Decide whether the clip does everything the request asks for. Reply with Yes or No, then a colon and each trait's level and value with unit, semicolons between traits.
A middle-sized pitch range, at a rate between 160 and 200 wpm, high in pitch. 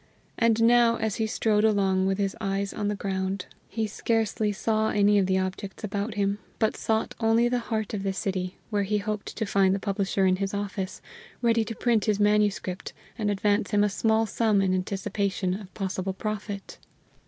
No: narrow, 2.1 semitones; average, 190 wpm; high, 205 Hz